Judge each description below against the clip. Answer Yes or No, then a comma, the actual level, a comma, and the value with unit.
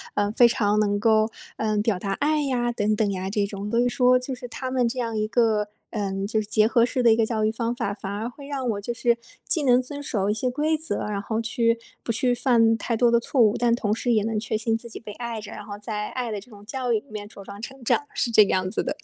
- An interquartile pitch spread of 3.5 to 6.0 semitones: No, average, 2.7 semitones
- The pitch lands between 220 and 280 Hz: Yes, high, 225 Hz